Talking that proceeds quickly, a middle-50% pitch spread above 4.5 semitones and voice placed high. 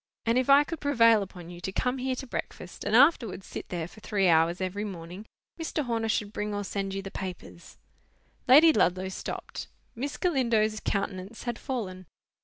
No: average, 185 wpm; average, 5.2 semitones; high, 210 Hz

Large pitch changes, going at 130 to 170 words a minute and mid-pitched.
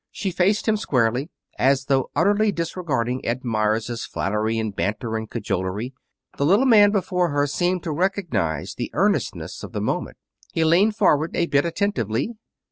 Yes: wide, 8.4 semitones; average, 160 wpm; medium, 145 Hz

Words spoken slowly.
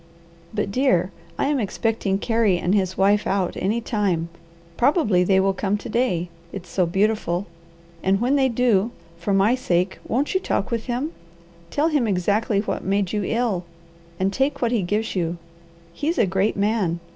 No: average, 175 wpm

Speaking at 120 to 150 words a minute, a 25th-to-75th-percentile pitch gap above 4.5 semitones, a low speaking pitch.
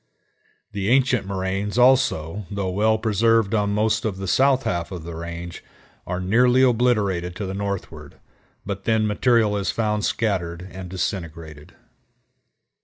No: average, 140 wpm; average, 3.6 semitones; low, 100 Hz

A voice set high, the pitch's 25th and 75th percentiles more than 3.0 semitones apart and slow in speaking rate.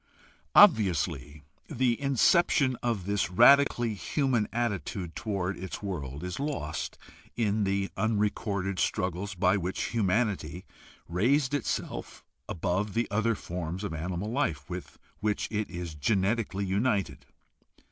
No: low, 100 Hz; average, 4.5 semitones; slow, 115 wpm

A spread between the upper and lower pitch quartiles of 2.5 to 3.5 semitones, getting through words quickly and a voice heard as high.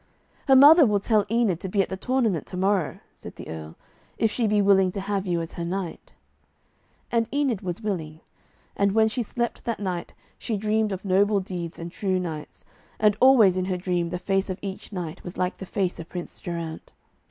Yes: average, 3.2 semitones; fast, 210 wpm; high, 195 Hz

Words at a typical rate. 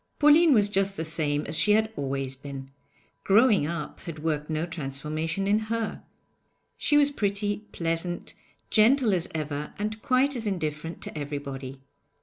Yes: average, 150 wpm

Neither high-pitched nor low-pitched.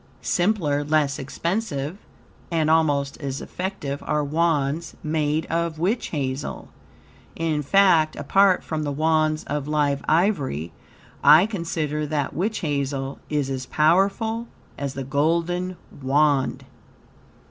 Yes: medium, 155 Hz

